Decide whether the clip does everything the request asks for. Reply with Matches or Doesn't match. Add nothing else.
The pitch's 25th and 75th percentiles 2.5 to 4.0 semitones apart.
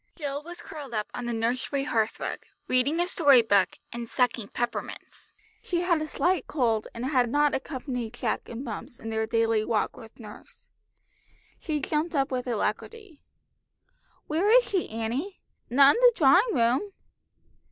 Doesn't match